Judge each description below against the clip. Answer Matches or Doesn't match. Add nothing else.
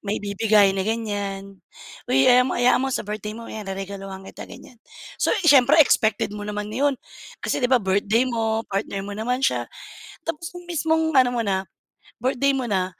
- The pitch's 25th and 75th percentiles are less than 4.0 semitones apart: Doesn't match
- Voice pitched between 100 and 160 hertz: Doesn't match